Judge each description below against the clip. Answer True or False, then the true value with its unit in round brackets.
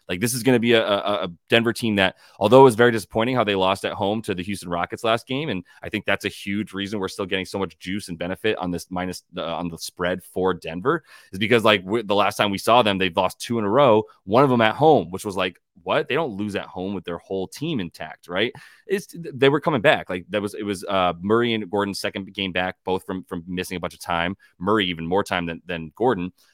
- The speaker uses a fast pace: True (270 wpm)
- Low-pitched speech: True (100 Hz)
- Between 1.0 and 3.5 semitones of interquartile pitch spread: True (3.2 semitones)